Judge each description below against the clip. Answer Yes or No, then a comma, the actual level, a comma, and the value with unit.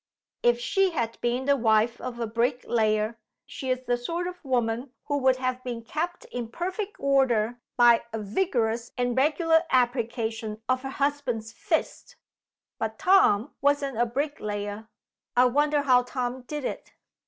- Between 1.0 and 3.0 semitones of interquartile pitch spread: No, average, 3.6 semitones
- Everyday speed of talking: Yes, average, 155 wpm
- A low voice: No, very high, 250 Hz